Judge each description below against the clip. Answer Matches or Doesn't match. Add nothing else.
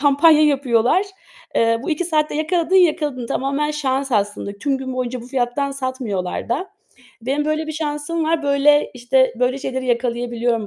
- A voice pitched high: Matches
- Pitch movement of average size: Matches